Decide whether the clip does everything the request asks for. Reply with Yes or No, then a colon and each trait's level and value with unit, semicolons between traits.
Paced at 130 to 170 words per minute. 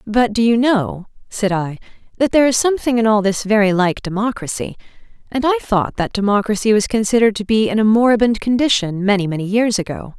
No: average, 195 wpm